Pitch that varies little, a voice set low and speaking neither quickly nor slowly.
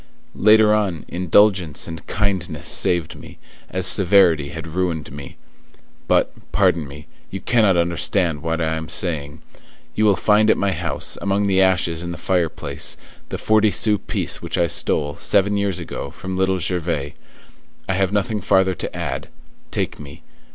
No: average, 3.5 semitones; very low, 90 Hz; average, 160 wpm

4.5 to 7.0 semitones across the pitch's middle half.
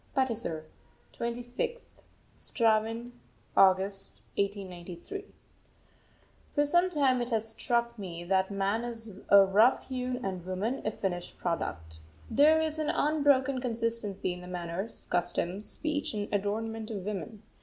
Yes: average, 4.8 semitones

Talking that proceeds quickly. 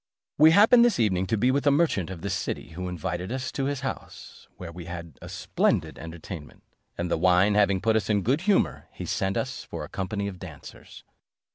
Yes: fast, 210 wpm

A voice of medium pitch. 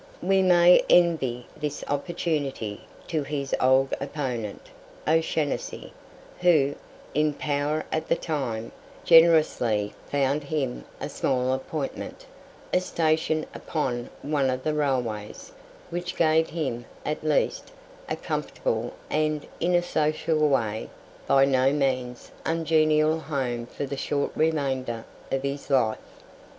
Yes: medium, 145 Hz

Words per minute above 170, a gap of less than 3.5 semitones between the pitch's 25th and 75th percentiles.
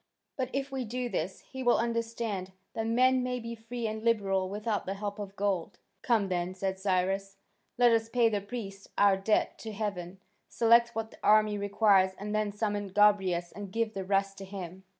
Yes: average, 190 wpm; average, 2.9 semitones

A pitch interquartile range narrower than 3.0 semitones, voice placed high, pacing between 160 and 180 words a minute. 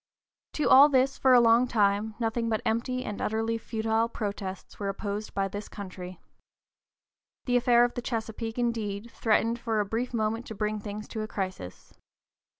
Yes: narrow, 2.4 semitones; high, 225 Hz; average, 170 wpm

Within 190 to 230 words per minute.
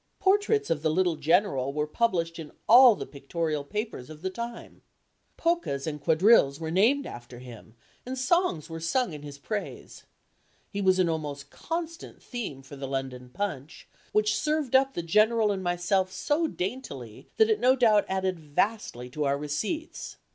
No: average, 170 wpm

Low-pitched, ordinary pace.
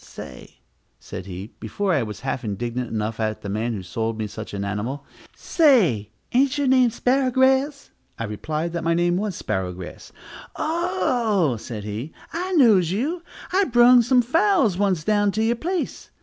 No: medium, 180 Hz; average, 170 wpm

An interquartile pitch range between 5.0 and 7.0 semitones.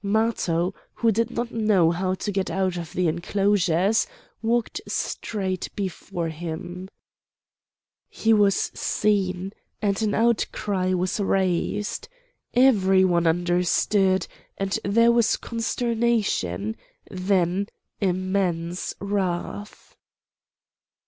No: average, 3.0 semitones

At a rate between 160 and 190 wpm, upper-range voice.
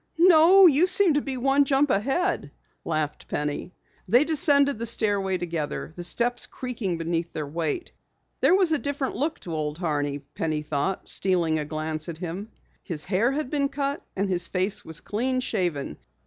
Yes: average, 175 wpm; high, 195 Hz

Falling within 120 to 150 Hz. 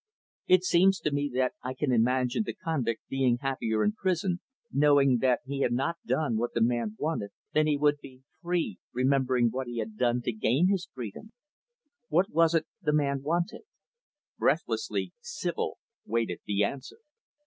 Yes: low, 135 Hz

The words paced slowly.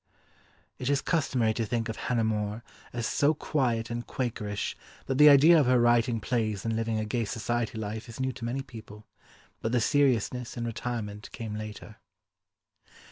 No: average, 175 wpm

